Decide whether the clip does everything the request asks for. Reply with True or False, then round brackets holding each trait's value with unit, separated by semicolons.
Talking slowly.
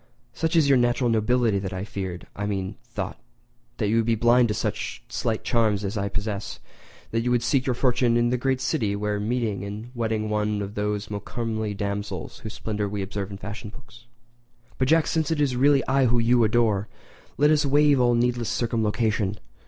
False (200 wpm)